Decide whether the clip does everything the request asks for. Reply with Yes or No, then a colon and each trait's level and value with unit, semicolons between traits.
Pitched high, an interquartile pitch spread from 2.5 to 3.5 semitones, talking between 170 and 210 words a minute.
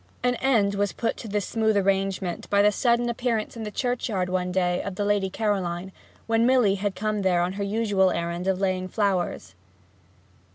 Yes: high, 200 Hz; average, 2.9 semitones; average, 190 wpm